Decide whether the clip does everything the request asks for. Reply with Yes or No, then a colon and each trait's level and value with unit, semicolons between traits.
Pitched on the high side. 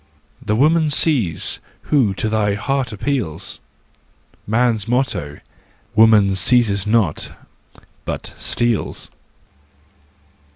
No: low, 110 Hz